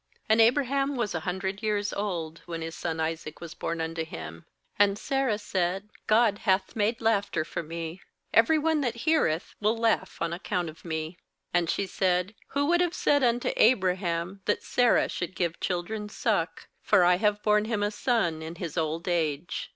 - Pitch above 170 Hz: Yes, high, 190 Hz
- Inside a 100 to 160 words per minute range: No, average, 180 wpm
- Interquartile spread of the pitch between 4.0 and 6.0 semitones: Yes, average, 5.0 semitones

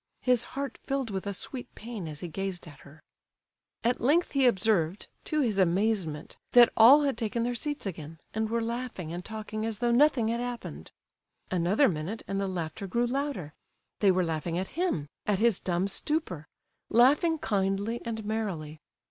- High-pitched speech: Yes, high, 215 Hz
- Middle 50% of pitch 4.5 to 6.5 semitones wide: Yes, average, 5.2 semitones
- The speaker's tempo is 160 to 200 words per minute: Yes, average, 170 wpm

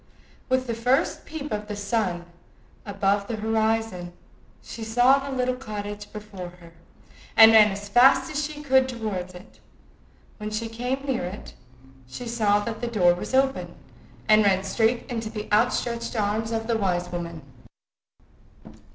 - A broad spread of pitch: No, average, 3.2 semitones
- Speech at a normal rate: Yes, average, 160 wpm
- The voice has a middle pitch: No, high, 220 Hz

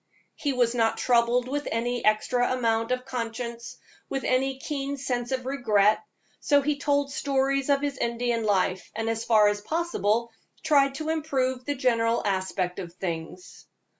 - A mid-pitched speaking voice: No, high, 245 Hz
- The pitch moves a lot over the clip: No, average, 3.4 semitones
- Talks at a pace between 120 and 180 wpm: Yes, average, 160 wpm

